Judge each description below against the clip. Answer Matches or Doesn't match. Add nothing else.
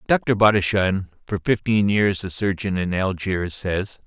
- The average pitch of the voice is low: Matches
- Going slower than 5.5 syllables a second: Matches